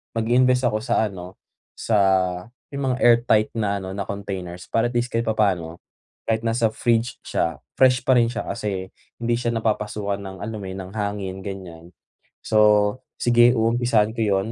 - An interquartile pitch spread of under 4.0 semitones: Yes, average, 3.2 semitones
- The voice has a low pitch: Yes, low, 110 Hz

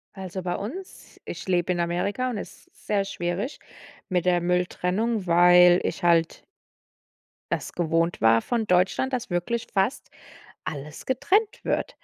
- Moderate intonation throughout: Yes, average, 4.0 semitones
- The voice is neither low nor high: Yes, medium, 180 Hz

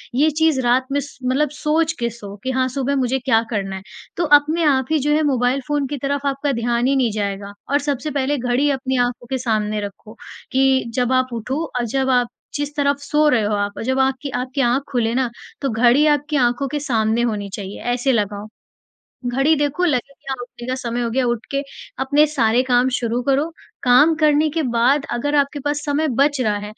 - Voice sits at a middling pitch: No, very high, 260 Hz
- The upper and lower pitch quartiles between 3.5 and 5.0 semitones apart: No, average, 3.1 semitones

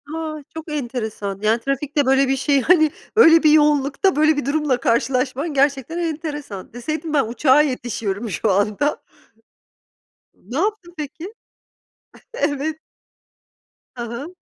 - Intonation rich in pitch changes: No, average, 4.2 semitones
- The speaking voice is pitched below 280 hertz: No, very high, 285 Hz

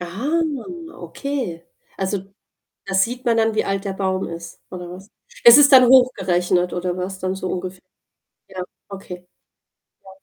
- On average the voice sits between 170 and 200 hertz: Yes, high, 190 Hz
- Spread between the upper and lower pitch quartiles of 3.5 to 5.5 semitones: Yes, average, 4.1 semitones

